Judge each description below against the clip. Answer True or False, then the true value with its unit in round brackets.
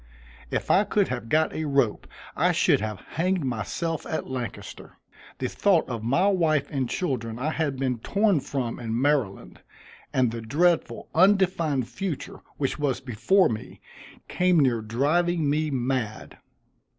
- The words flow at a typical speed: True (150 wpm)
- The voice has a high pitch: False (140 Hz)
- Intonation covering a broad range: True (5.9 semitones)